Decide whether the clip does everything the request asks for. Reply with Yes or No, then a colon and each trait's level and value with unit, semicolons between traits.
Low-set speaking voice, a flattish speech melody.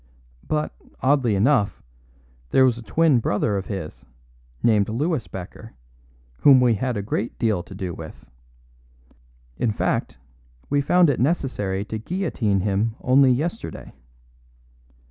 No: low, 115 Hz; wide, 5.4 semitones